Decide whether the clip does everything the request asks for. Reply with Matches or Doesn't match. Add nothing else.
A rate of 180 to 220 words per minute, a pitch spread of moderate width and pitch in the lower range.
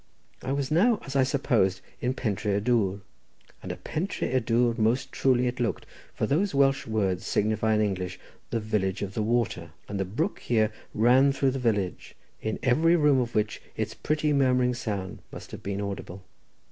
Matches